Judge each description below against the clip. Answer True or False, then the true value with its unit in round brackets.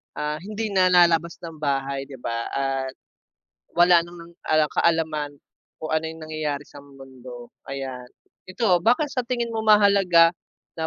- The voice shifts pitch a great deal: False (4.8 semitones)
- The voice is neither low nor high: True (160 Hz)